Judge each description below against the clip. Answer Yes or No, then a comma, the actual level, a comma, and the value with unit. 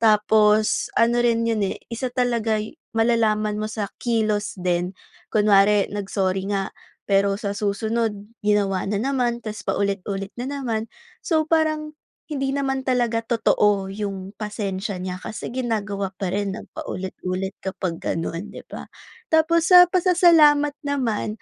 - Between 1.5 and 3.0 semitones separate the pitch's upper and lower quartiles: No, average, 3.7 semitones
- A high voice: Yes, high, 215 Hz